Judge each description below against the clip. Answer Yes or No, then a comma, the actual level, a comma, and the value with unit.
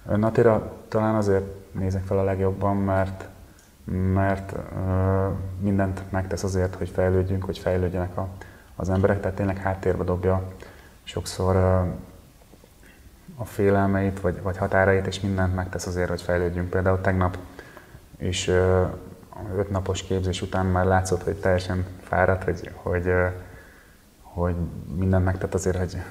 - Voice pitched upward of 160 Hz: No, very low, 95 Hz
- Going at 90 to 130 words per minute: Yes, average, 120 wpm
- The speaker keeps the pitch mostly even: Yes, narrow, 1.0 semitones